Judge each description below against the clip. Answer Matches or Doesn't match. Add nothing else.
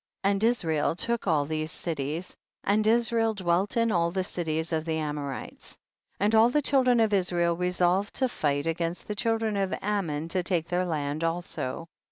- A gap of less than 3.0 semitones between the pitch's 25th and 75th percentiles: Doesn't match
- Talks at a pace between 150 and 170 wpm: Doesn't match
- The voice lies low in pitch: Doesn't match